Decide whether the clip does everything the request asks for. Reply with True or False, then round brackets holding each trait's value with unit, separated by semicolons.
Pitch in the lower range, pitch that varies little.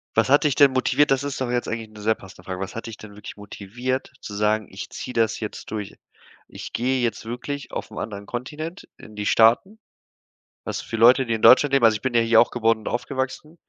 False (115 Hz; 3.4 semitones)